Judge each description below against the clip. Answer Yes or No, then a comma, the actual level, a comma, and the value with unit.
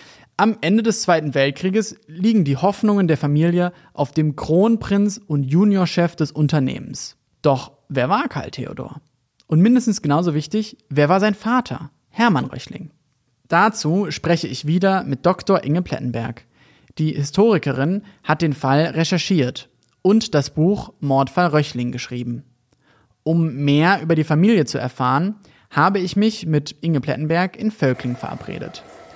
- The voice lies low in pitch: No, medium, 160 Hz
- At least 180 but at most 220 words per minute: No, average, 140 wpm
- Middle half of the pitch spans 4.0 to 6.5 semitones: Yes, wide, 5.4 semitones